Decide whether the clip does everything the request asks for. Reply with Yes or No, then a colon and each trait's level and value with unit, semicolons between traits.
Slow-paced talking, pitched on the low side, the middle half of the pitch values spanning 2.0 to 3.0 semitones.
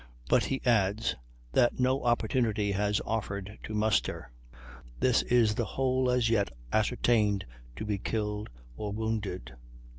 Yes: slow, 130 wpm; low, 110 Hz; average, 2.7 semitones